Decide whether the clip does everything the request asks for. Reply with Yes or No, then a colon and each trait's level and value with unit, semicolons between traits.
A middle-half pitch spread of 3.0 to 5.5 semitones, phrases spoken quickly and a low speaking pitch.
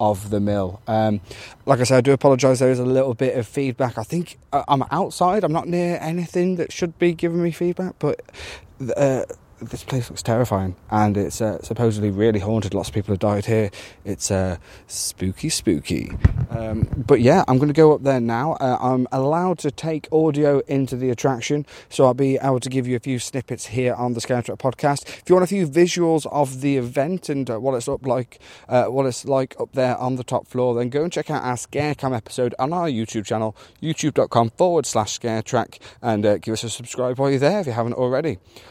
Yes: average, 4.3 semitones; fast, 225 wpm; low, 130 Hz